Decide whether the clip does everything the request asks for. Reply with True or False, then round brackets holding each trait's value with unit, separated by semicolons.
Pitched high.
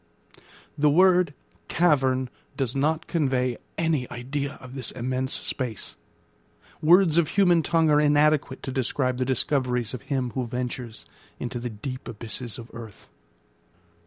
False (130 Hz)